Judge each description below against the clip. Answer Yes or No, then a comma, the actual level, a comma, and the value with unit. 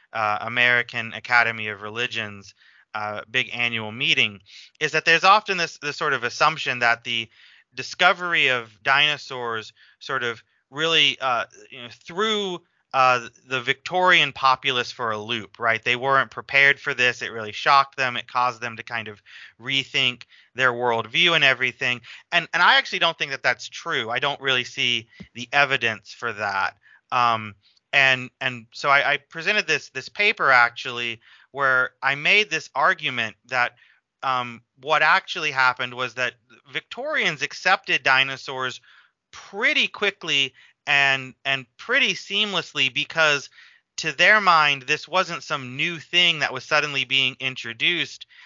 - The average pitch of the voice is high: No, low, 130 Hz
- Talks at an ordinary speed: Yes, average, 150 wpm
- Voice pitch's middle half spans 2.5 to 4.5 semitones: Yes, average, 3.8 semitones